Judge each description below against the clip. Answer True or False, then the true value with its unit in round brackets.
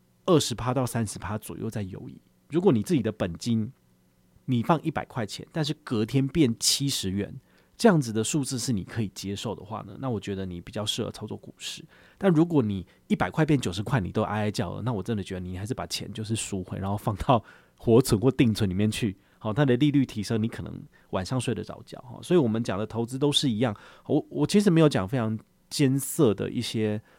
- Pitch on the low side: True (115 Hz)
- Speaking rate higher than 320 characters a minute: True (330 characters per minute)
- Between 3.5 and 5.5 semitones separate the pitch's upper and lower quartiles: True (5.0 semitones)